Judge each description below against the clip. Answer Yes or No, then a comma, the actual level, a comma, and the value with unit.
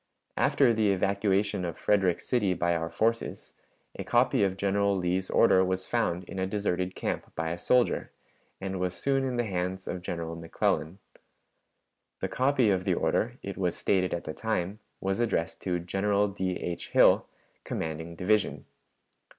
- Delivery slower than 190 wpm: Yes, average, 165 wpm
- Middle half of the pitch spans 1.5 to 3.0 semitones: Yes, average, 2.7 semitones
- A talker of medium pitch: No, very low, 95 Hz